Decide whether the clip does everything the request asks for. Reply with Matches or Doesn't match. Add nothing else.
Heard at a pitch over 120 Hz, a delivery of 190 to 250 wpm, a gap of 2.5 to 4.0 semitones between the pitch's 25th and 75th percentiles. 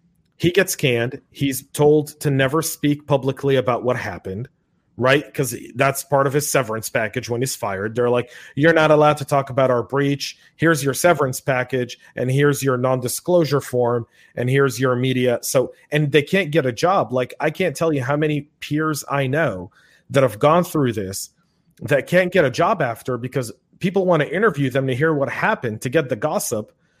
Matches